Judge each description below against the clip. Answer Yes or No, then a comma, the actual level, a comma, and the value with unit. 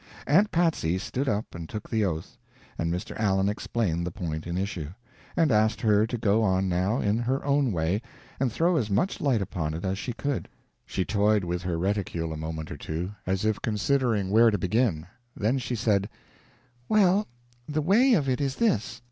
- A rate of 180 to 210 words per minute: Yes, average, 195 wpm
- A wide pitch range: Yes, wide, 5.9 semitones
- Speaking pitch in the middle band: No, low, 105 Hz